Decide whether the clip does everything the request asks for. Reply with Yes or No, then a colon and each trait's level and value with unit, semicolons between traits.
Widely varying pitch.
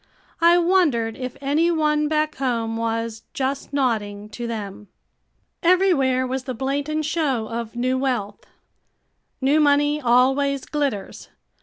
No: average, 4.6 semitones